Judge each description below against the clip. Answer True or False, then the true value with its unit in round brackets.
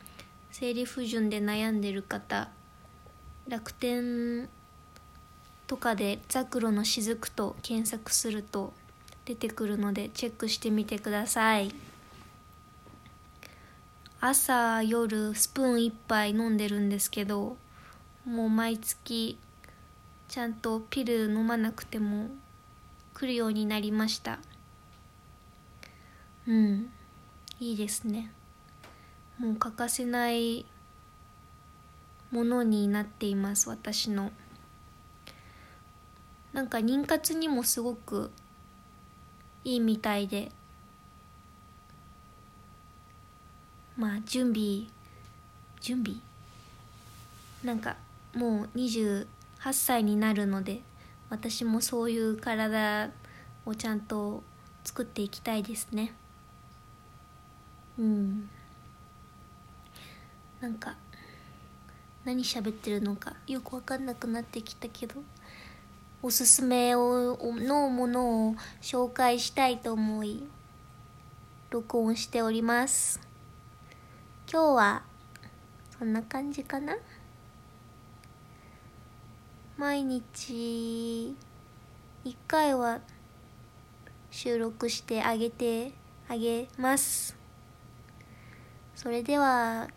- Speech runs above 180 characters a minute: False (165 characters per minute)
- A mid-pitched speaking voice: False (220 Hz)